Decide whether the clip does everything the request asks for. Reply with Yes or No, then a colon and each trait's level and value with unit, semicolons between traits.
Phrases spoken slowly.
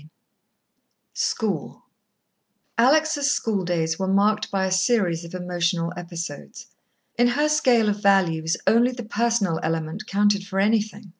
Yes: slow, 130 wpm